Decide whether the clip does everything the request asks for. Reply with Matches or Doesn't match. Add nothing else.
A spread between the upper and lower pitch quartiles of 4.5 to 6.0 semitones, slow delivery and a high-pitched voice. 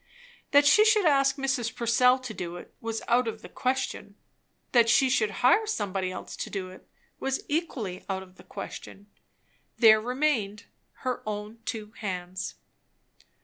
Doesn't match